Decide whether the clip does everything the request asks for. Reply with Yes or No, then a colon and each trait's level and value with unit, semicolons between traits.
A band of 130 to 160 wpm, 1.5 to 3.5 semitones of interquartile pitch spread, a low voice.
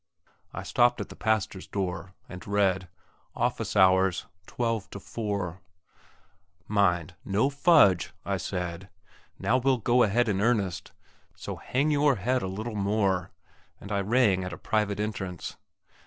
No: average, 140 wpm; average, 4.0 semitones; low, 100 Hz